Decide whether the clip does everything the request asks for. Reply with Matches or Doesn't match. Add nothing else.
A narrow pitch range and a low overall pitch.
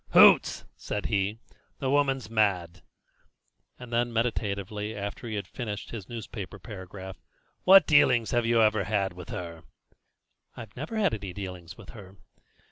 Doesn't match